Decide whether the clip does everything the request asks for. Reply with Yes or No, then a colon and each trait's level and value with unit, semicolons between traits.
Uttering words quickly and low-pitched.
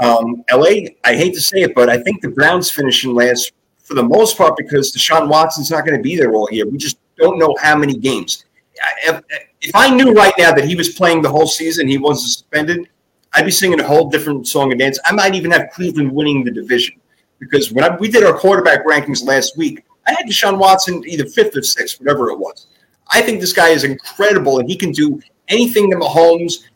No: fast, 230 wpm; medium, 165 Hz